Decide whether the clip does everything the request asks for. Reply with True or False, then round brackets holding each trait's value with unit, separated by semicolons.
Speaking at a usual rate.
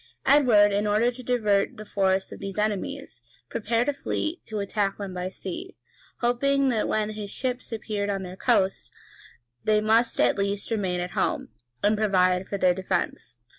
True (170 wpm)